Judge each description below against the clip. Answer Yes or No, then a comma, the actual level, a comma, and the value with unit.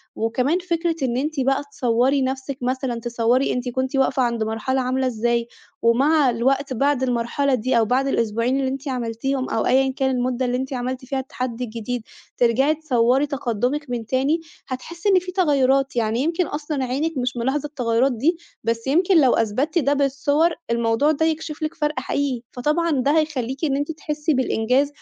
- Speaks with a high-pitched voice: Yes, very high, 265 Hz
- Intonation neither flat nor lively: Yes, average, 3.0 semitones